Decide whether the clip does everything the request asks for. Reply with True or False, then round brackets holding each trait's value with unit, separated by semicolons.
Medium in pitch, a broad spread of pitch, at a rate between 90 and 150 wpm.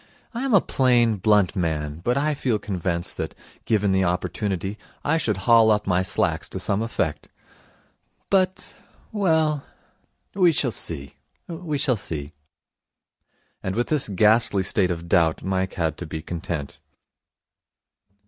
False (105 Hz; 7.2 semitones; 140 wpm)